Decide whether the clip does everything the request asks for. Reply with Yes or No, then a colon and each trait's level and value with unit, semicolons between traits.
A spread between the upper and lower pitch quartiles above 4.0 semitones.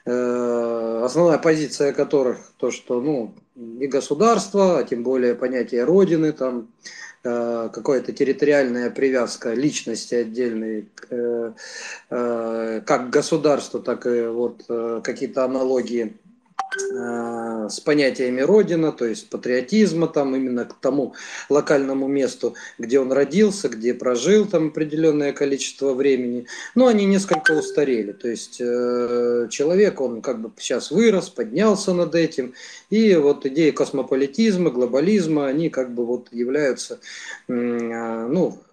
Yes: wide, 5.4 semitones